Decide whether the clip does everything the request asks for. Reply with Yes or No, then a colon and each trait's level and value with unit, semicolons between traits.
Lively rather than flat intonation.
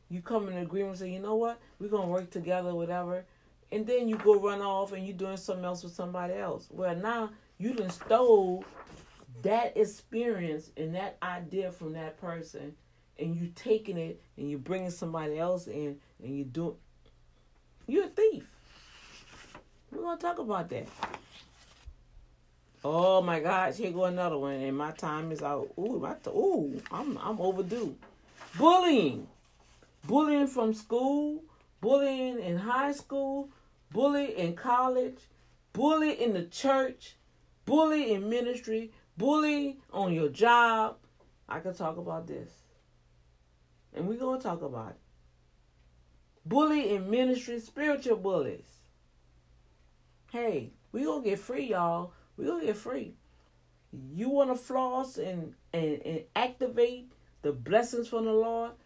Yes: wide, 7.4 semitones